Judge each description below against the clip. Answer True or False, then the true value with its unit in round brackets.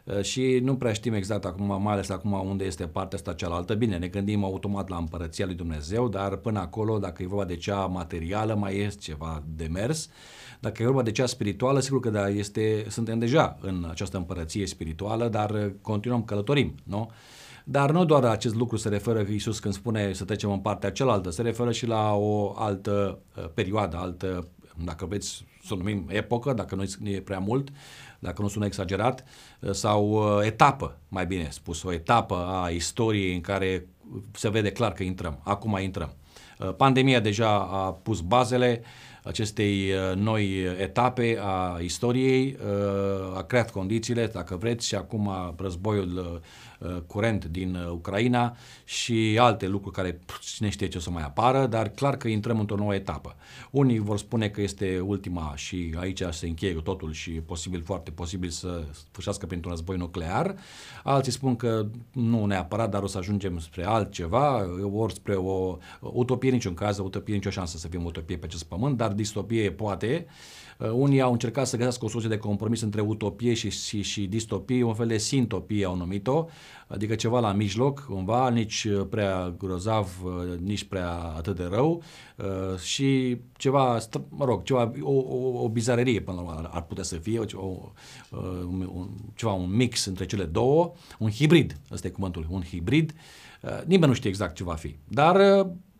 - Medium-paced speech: False (180 wpm)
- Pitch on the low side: True (100 Hz)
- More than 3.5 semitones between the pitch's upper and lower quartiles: True (4.0 semitones)